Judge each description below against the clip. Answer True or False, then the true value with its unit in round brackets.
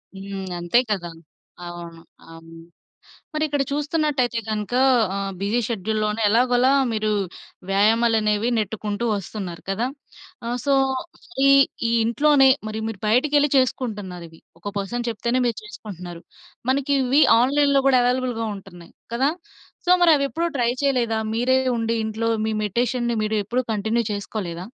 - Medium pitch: False (225 Hz)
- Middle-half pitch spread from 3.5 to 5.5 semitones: True (4.1 semitones)